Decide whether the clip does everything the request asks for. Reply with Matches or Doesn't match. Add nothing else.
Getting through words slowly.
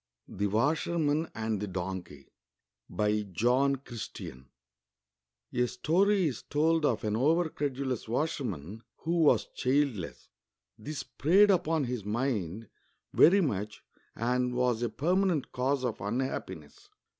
Matches